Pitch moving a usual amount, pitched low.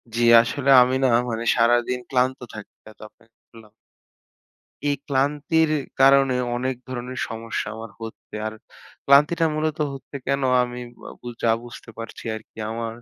Yes: average, 3.2 semitones; low, 125 Hz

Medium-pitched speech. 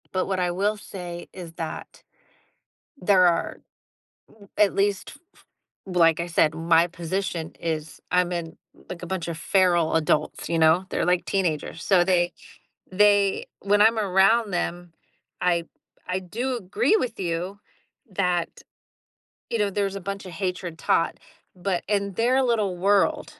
Yes: medium, 180 Hz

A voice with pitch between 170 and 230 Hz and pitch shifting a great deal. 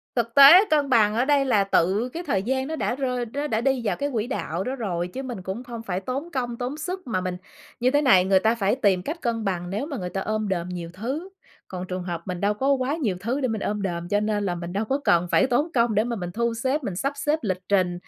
Yes: high, 225 Hz; wide, 5.9 semitones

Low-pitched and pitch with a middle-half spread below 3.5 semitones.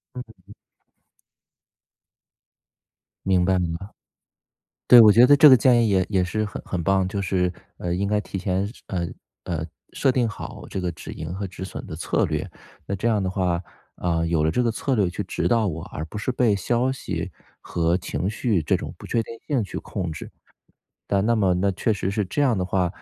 No: very low, 95 Hz; average, 3.9 semitones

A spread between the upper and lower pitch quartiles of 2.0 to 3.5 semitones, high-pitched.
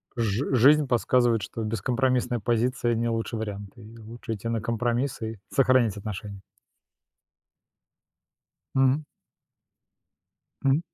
No: narrow, 2.4 semitones; low, 115 Hz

